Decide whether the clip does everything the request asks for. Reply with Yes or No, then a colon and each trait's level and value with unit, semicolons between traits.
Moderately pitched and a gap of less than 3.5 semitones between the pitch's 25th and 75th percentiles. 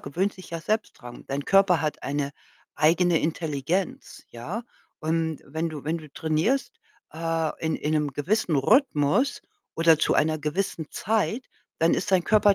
No: medium, 160 Hz; average, 4.2 semitones